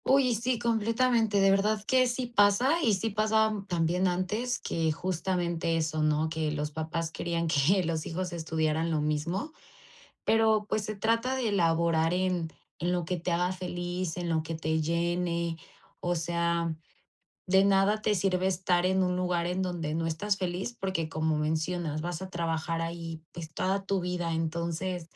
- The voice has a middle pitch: Yes, medium, 175 Hz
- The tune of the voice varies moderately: Yes, average, 3.2 semitones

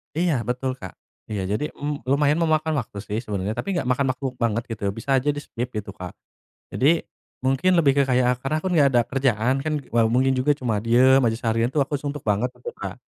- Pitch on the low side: Yes, low, 130 Hz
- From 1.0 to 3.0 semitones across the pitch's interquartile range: No, average, 4.0 semitones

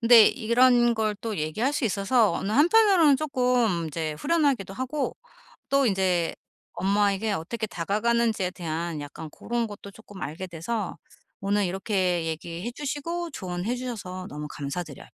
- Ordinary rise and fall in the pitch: No, wide, 5.7 semitones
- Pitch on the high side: Yes, high, 205 Hz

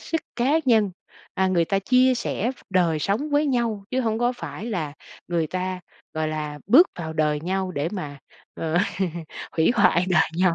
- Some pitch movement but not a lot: No, wide, 6.7 semitones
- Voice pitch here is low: No, medium, 185 Hz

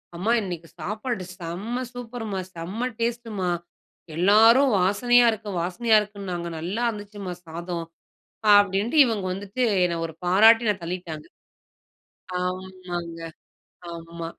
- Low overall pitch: No, high, 195 Hz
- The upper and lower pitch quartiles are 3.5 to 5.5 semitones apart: Yes, average, 4.4 semitones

